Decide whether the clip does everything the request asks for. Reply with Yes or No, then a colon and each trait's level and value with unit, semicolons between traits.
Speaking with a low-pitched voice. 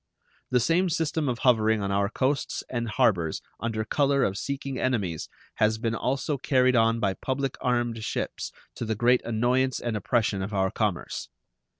Yes: low, 120 Hz